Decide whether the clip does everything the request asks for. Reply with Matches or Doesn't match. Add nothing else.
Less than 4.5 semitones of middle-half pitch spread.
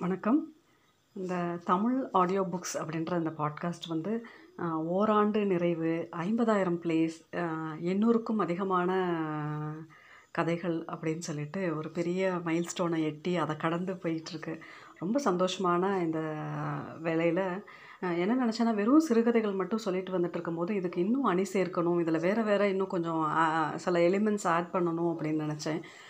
Matches